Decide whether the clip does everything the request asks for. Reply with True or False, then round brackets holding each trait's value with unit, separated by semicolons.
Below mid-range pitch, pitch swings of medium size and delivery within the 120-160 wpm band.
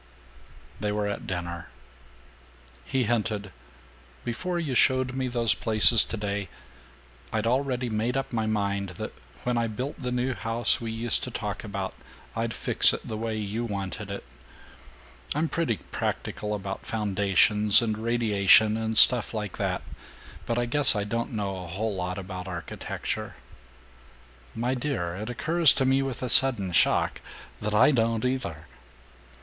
True (110 Hz; 3.3 semitones; 155 wpm)